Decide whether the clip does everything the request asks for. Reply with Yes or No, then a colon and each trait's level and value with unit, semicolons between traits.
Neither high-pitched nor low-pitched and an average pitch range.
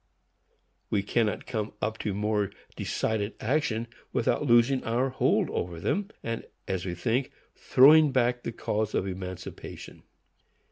No: low, 115 Hz; average, 3.7 semitones